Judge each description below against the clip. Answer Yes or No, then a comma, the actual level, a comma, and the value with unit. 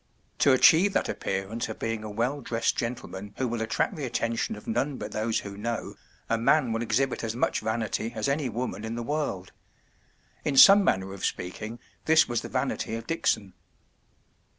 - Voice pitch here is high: No, low, 115 Hz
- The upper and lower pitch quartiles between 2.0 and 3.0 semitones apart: No, average, 3.4 semitones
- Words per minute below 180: No, average, 190 wpm